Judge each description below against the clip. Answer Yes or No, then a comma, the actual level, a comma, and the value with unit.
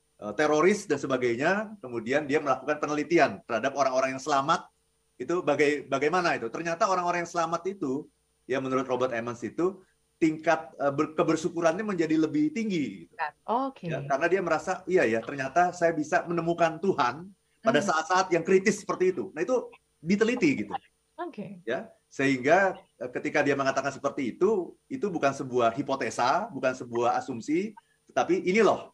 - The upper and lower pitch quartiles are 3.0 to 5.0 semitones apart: No, wide, 5.5 semitones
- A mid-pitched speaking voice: Yes, medium, 165 Hz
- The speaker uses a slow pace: No, fast, 140 wpm